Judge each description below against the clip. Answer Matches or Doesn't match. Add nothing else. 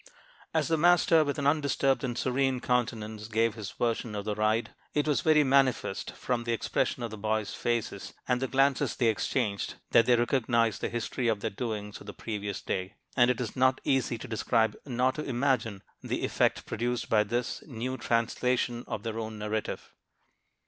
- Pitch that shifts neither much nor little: Matches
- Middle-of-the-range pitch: Doesn't match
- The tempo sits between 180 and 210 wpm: Matches